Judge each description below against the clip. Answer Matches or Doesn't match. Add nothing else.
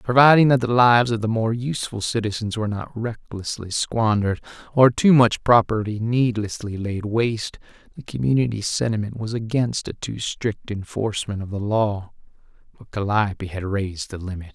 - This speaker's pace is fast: Doesn't match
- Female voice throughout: Doesn't match